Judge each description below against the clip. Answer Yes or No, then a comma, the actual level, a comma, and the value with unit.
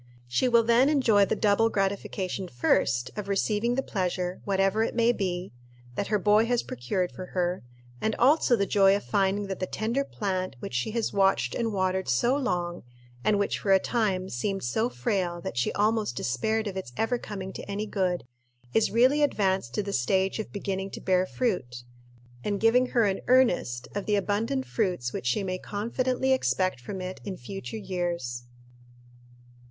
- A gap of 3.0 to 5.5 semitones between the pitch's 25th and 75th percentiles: Yes, average, 3.4 semitones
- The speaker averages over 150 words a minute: Yes, average, 180 wpm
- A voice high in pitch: Yes, high, 200 Hz